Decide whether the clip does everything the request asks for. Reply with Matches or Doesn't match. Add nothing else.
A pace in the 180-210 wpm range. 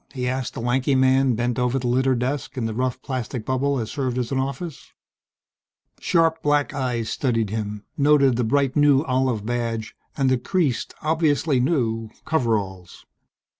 Doesn't match